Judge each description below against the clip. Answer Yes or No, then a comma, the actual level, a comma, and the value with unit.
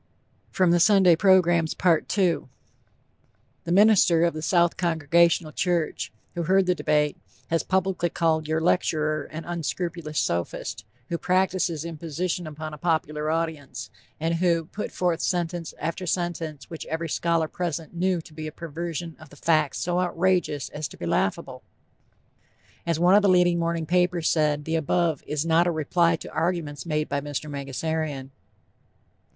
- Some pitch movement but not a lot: No, narrow, 2.2 semitones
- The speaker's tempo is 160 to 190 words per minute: No, average, 145 wpm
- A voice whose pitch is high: No, medium, 165 Hz